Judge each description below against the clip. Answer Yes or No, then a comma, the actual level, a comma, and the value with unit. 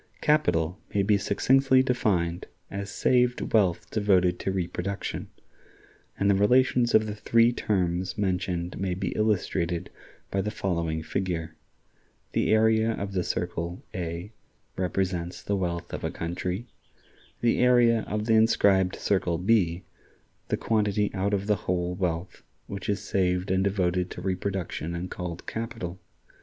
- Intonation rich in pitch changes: No, average, 3.2 semitones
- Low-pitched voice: Yes, very low, 95 Hz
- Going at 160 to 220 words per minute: No, average, 140 wpm